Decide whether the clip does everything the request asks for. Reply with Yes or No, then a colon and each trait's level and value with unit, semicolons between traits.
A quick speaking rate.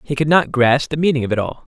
Yes: fast, 310 wpm